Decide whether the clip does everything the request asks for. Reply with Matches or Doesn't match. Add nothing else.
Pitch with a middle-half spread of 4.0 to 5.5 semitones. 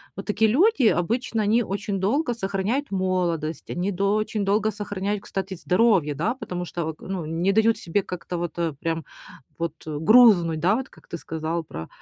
Matches